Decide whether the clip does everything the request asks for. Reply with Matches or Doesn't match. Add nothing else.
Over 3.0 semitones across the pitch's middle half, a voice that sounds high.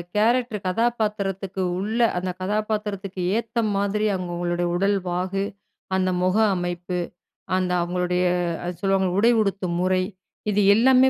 Doesn't match